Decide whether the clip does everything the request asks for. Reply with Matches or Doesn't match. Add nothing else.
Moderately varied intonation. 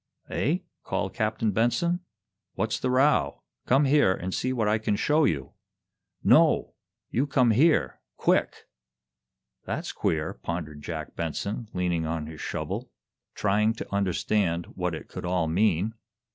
Doesn't match